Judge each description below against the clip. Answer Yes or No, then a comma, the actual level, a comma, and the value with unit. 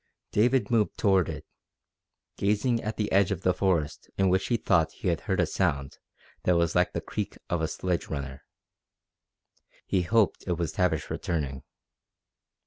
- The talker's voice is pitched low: Yes, very low, 90 Hz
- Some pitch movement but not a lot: Yes, average, 4.1 semitones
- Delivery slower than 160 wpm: No, average, 165 wpm